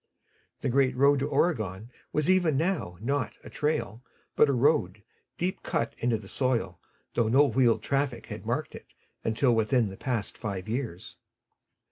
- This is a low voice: Yes, low, 125 Hz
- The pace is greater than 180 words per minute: No, average, 160 wpm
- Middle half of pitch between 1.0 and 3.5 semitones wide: No, average, 4.4 semitones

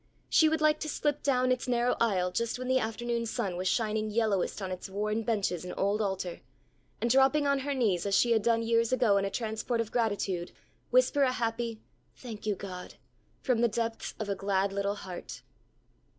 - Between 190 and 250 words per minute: Yes, average, 200 wpm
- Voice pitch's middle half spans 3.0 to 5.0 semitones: Yes, average, 3.7 semitones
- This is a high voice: Yes, high, 225 Hz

